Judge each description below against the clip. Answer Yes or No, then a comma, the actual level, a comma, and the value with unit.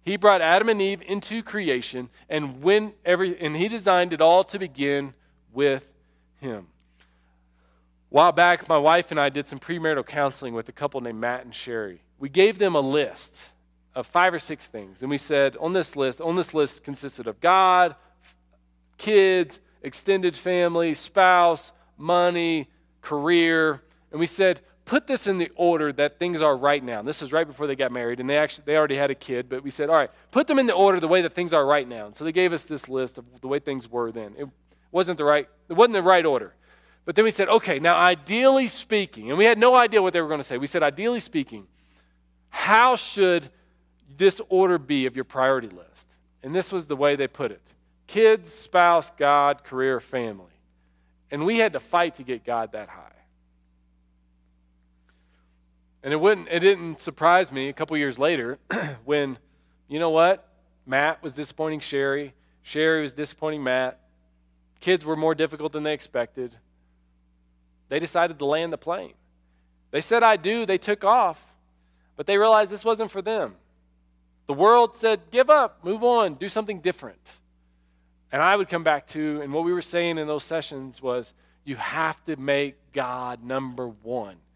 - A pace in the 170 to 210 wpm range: Yes, average, 190 wpm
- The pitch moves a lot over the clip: Yes, wide, 7.1 semitones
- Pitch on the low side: No, medium, 150 Hz